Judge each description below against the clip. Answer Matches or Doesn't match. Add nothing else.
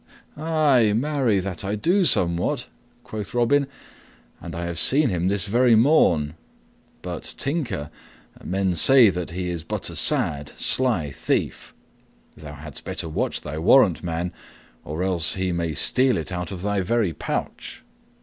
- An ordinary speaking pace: Matches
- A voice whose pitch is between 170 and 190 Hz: Doesn't match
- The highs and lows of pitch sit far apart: Matches